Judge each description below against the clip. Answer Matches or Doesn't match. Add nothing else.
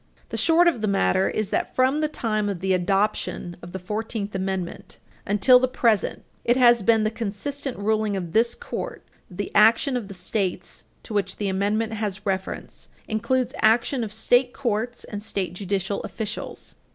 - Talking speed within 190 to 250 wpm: Doesn't match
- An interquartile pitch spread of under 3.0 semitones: Doesn't match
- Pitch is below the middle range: Doesn't match